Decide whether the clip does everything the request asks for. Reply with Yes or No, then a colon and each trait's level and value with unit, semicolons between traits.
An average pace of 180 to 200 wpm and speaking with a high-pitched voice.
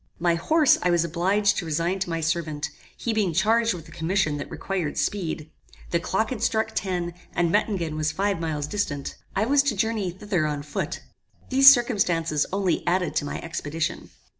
No: average, 185 wpm; medium, 175 Hz